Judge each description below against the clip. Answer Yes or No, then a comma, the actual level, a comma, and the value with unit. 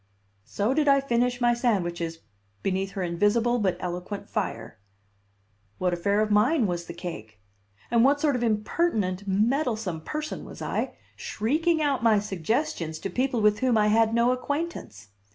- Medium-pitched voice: No, high, 215 Hz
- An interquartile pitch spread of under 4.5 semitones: No, wide, 5.4 semitones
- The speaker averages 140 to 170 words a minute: Yes, average, 155 wpm